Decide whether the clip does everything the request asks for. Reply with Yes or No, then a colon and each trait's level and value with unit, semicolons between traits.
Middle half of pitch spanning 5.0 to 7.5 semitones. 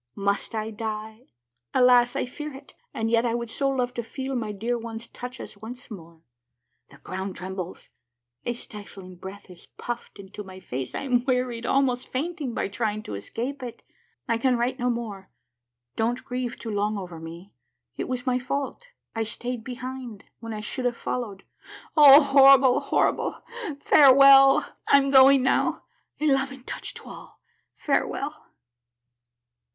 No: average, 3.8 semitones